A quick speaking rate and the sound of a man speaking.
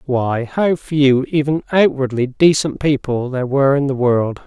No: average, 160 wpm; male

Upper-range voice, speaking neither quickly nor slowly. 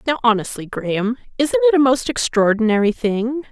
Yes: high, 230 Hz; average, 155 wpm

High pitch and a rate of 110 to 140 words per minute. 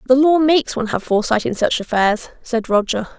No: high, 240 Hz; fast, 205 wpm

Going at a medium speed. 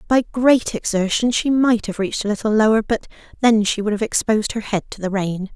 No: fast, 225 wpm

